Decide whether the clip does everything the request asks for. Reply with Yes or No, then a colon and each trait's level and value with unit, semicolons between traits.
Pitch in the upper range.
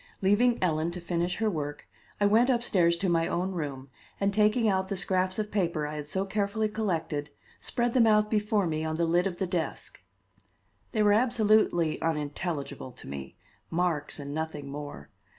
No: medium, 180 Hz